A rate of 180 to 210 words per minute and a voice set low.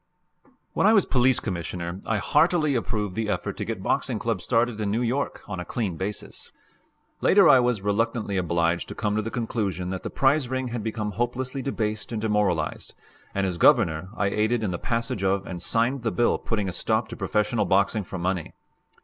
Yes: average, 200 wpm; low, 110 Hz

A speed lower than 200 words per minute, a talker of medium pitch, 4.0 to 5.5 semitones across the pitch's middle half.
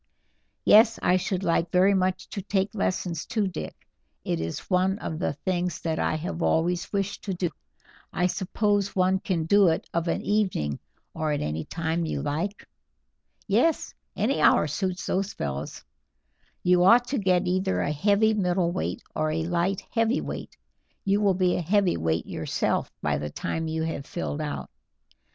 No: average, 165 wpm; medium, 180 Hz; average, 3.5 semitones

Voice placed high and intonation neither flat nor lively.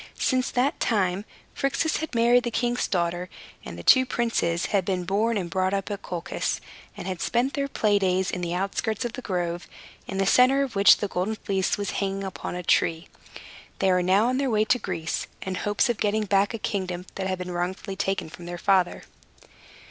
Yes: high, 195 Hz; average, 4.1 semitones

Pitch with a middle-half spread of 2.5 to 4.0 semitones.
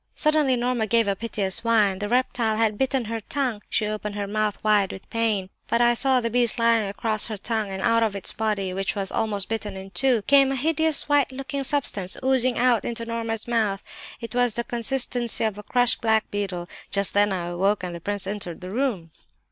Yes: average, 3.4 semitones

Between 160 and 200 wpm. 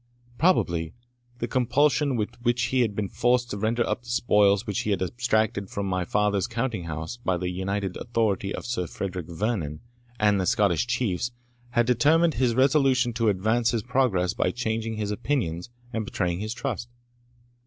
Yes: average, 175 wpm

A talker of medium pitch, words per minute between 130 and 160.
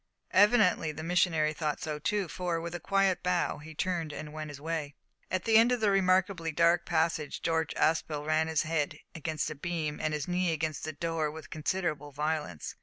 No: medium, 160 Hz; average, 195 wpm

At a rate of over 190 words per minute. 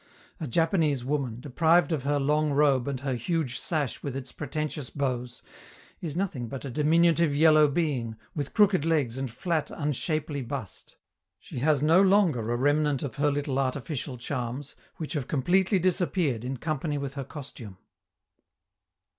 No: average, 155 wpm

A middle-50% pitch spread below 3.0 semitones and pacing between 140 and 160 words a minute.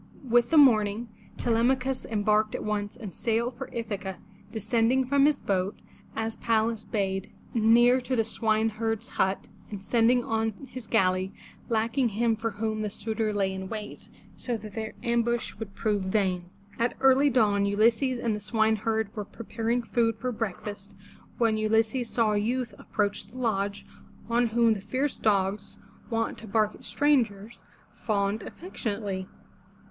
Yes: narrow, 2.4 semitones; average, 155 wpm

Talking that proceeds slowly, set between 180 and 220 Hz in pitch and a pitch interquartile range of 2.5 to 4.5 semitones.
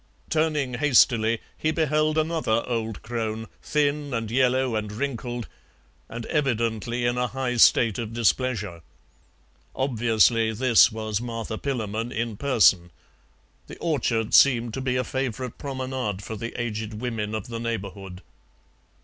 No: slow, 130 wpm; low, 120 Hz; average, 2.9 semitones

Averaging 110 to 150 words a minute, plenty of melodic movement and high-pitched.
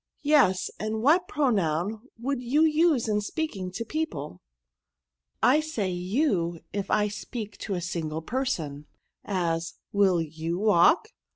Yes: average, 145 wpm; wide, 7.5 semitones; high, 205 Hz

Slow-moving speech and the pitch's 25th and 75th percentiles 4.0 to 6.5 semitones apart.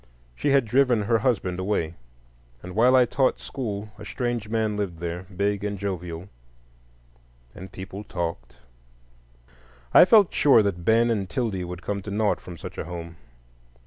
No: average, 160 wpm; average, 4.3 semitones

